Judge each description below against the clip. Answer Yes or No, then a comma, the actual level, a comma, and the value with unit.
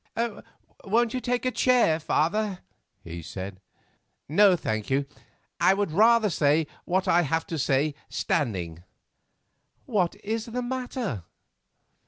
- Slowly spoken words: Yes, slow, 125 wpm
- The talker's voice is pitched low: No, medium, 175 Hz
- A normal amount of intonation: No, wide, 8.1 semitones